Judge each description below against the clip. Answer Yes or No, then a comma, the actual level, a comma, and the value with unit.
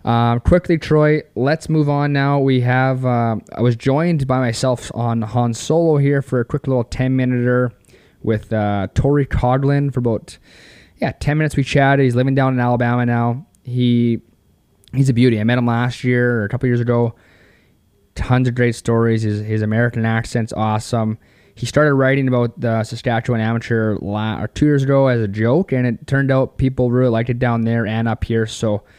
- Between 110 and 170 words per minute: No, average, 190 wpm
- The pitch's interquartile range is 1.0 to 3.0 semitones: Yes, average, 2.7 semitones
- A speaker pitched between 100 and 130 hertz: Yes, low, 120 Hz